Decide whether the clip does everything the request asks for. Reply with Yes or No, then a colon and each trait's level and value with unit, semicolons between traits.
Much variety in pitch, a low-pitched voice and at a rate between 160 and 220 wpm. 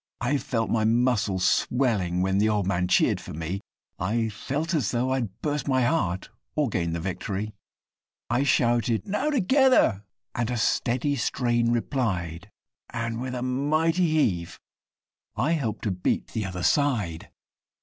No: wide, 5.8 semitones; low, 115 Hz; average, 150 wpm